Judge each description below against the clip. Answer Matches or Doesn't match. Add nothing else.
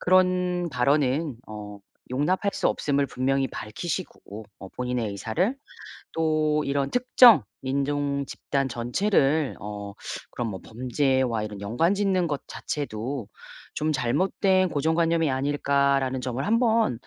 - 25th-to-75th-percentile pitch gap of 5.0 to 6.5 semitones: Matches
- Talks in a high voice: Doesn't match